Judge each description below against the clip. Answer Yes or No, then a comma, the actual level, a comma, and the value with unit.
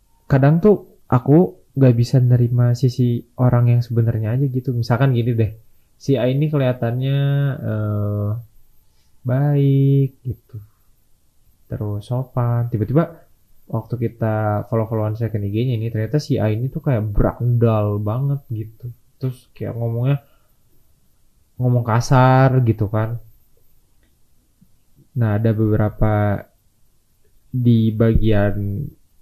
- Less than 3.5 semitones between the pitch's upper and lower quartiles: Yes, average, 3.0 semitones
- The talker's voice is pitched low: Yes, low, 120 Hz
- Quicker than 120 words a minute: No, average, 105 wpm